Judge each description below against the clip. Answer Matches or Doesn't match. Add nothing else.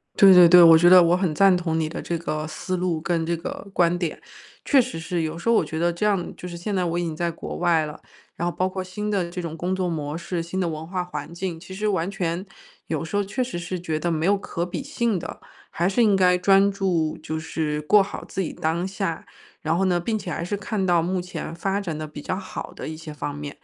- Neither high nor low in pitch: Matches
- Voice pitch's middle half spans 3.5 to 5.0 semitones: Doesn't match